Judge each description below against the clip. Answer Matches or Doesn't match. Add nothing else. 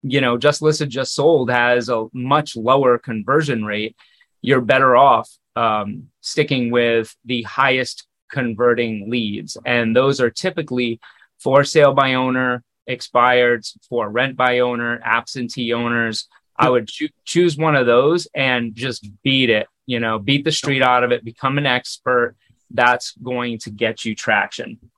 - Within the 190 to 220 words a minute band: Doesn't match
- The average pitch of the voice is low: Matches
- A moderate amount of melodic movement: Doesn't match